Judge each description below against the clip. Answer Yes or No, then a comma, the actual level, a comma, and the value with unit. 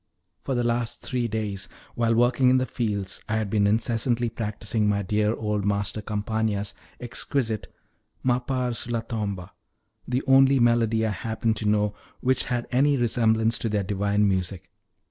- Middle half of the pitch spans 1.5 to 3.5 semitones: Yes, narrow, 2.6 semitones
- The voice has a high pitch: No, low, 110 Hz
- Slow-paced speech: No, average, 155 wpm